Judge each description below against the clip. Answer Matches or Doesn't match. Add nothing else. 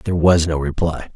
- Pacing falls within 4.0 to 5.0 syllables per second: Doesn't match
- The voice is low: Matches